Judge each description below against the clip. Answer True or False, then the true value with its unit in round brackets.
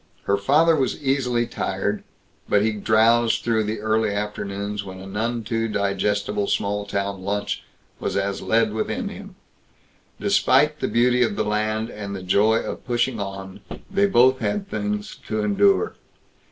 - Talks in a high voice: False (110 Hz)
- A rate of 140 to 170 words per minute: True (155 wpm)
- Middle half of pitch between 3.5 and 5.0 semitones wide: False (3.1 semitones)